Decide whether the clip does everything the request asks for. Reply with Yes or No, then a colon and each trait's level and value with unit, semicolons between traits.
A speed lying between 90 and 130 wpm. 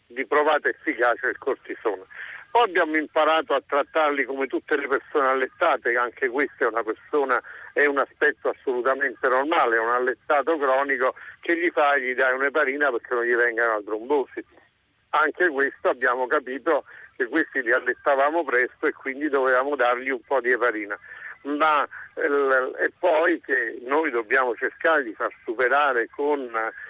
No: average, 155 wpm